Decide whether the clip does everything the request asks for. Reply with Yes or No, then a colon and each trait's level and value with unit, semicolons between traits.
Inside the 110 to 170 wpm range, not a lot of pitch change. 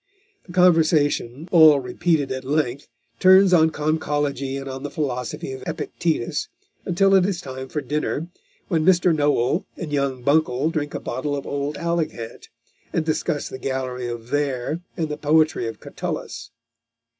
No: average, 155 wpm; average, 3.5 semitones